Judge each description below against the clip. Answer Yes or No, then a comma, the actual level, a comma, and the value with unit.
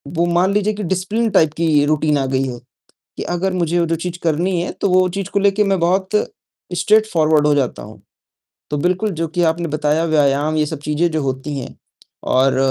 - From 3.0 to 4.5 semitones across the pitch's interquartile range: Yes, average, 3.7 semitones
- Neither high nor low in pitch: Yes, medium, 165 Hz